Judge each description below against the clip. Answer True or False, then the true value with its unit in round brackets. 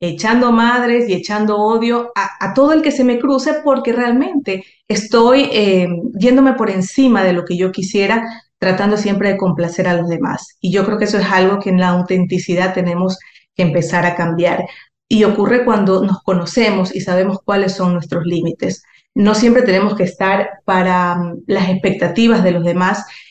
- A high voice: True (195 Hz)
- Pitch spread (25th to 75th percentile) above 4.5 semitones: False (3.9 semitones)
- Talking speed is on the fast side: False (180 wpm)